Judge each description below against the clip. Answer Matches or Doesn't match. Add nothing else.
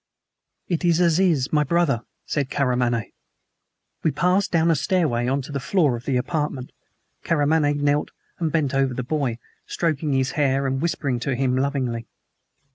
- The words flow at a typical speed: Matches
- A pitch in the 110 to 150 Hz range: Matches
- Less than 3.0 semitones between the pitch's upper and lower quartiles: Doesn't match